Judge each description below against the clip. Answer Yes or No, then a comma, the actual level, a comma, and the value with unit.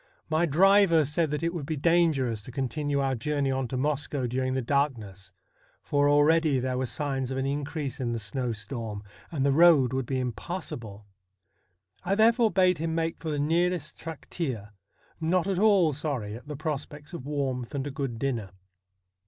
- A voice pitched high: No, medium, 145 Hz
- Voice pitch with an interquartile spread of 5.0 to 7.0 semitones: No, average, 4.0 semitones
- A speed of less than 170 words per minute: No, average, 175 wpm